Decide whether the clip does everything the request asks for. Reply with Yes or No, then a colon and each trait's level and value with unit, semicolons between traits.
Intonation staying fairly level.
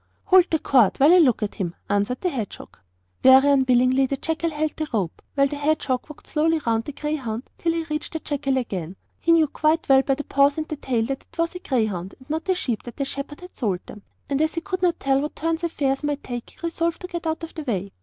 No: average, 4.3 semitones